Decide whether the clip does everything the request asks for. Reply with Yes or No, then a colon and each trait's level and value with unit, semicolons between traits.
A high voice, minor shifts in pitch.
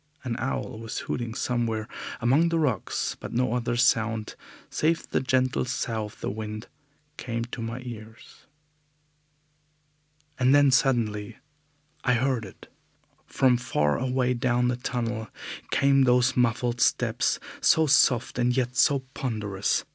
No: low, 120 Hz; narrow, 2.2 semitones